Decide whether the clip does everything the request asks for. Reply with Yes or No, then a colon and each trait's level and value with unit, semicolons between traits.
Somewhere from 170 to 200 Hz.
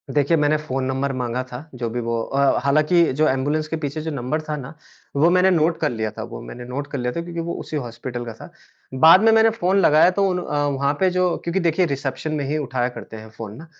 No: medium, 145 Hz